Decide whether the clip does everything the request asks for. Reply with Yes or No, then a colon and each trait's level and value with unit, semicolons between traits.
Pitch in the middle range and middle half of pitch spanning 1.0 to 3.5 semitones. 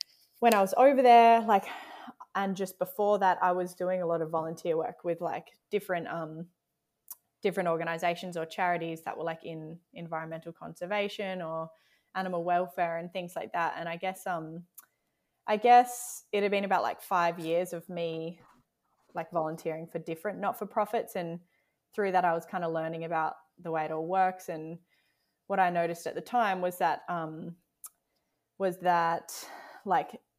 Yes: medium, 175 Hz; average, 2.7 semitones